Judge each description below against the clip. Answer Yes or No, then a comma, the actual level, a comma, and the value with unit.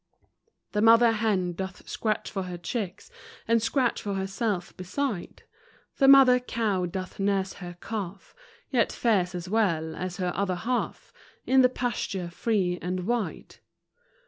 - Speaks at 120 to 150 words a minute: Yes, average, 145 wpm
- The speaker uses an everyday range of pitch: Yes, average, 4.2 semitones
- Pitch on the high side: Yes, high, 200 Hz